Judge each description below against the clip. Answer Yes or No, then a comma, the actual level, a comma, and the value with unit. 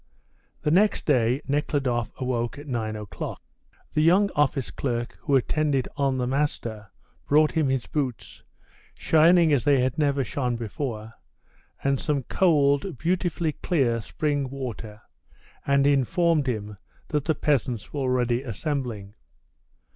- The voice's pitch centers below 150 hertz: Yes, low, 135 Hz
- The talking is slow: Yes, slow, 130 wpm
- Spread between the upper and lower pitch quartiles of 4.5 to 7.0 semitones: No, average, 3.8 semitones